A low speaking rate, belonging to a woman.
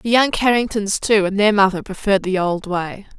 No: fast, 205 wpm; female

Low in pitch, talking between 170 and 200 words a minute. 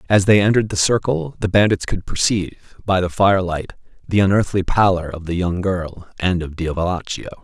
Yes: very low, 95 Hz; average, 180 wpm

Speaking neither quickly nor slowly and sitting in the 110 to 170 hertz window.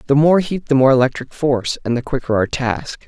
No: fast, 235 wpm; low, 135 Hz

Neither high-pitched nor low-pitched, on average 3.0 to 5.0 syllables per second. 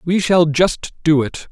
Yes: medium, 165 Hz; 3.7 syllables/s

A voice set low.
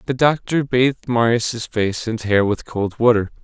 Yes: low, 115 Hz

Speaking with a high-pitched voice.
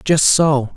No: medium, 145 Hz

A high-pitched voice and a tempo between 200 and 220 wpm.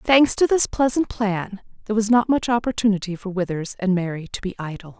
Yes: high, 210 Hz; fast, 205 wpm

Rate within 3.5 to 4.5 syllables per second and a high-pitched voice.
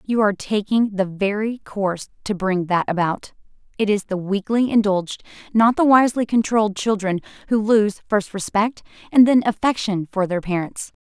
No: 5.1 syllables/s; high, 205 Hz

